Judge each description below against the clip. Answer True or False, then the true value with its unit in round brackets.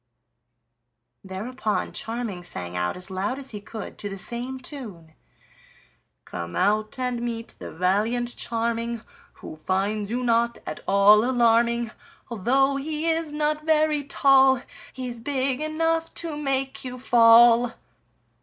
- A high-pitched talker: True (235 Hz)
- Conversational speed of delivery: False (130 wpm)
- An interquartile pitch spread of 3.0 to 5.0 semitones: True (4.3 semitones)